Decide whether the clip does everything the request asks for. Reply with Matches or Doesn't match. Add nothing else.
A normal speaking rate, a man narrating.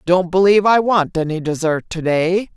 Doesn't match